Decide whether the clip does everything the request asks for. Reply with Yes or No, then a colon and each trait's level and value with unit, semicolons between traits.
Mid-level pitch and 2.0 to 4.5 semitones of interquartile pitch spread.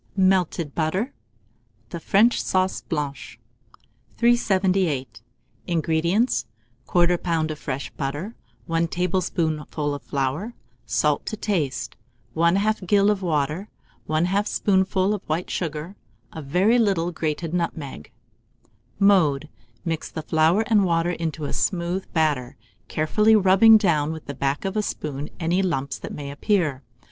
Yes: medium, 170 Hz; average, 4.2 semitones